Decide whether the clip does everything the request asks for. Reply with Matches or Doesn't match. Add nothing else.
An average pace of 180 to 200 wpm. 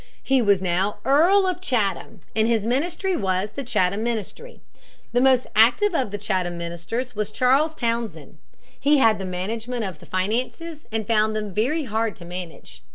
Doesn't match